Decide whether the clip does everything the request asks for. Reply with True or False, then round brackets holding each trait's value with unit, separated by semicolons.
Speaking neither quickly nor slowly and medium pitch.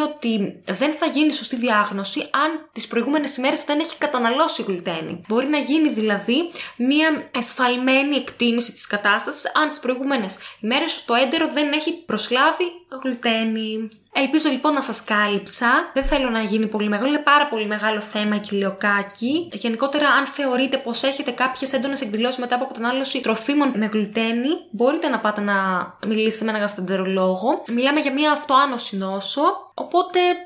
False (160 wpm; 255 Hz)